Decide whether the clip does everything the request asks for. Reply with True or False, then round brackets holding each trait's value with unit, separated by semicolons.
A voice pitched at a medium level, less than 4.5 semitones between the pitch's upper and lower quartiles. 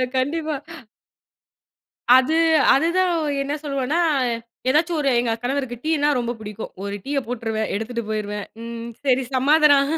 False (260 Hz; 4.1 semitones)